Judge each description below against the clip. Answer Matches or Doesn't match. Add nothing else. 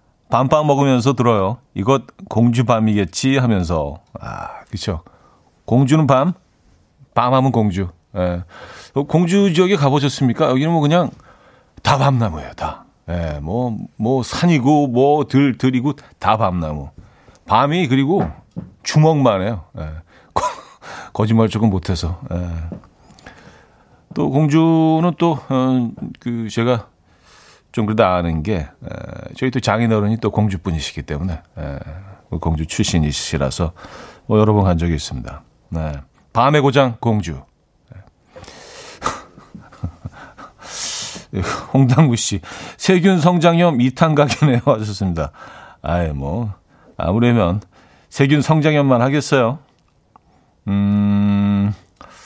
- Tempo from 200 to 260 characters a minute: Matches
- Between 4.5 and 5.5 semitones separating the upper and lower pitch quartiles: Doesn't match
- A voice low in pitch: Matches